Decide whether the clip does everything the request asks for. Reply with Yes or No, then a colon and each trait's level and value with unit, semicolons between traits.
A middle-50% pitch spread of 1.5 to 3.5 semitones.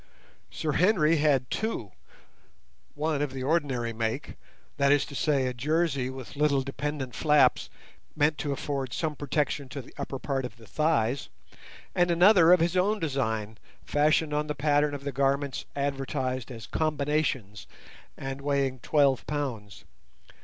Yes: narrow, 2.6 semitones